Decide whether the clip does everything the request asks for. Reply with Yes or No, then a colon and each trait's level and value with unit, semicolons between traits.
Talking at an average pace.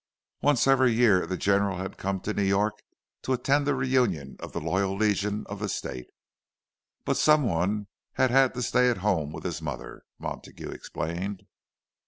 Yes: average, 175 wpm